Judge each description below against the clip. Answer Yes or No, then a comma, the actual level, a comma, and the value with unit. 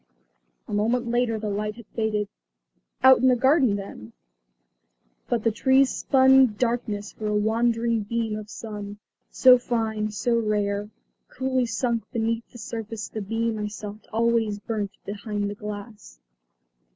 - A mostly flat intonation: Yes, narrow, 2.2 semitones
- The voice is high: Yes, high, 220 Hz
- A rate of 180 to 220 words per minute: No, average, 145 wpm